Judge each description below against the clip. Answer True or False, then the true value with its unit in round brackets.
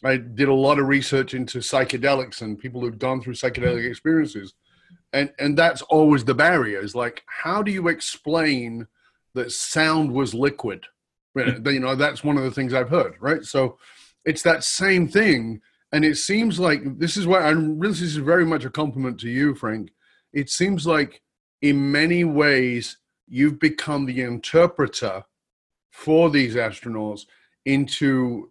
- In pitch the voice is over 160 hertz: False (140 Hz)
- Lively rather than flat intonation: False (3.8 semitones)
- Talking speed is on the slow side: False (165 wpm)